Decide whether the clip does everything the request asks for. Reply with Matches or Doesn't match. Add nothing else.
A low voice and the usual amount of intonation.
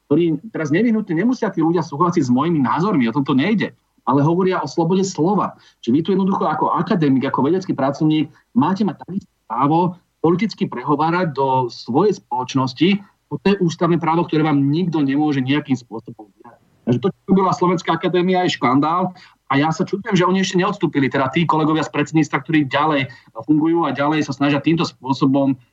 Doesn't match